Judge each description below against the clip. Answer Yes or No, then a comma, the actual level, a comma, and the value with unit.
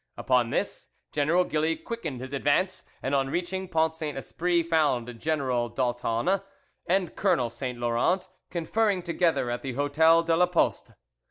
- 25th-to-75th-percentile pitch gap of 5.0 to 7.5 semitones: Yes, wide, 5.6 semitones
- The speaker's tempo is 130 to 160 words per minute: Yes, average, 150 wpm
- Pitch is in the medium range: Yes, medium, 155 Hz